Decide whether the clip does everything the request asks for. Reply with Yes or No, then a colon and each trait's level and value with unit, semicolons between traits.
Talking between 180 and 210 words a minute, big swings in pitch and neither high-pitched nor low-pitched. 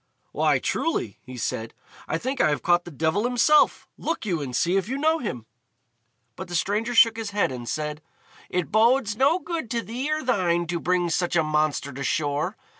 Yes: average, 200 wpm; wide, 7.8 semitones; medium, 180 Hz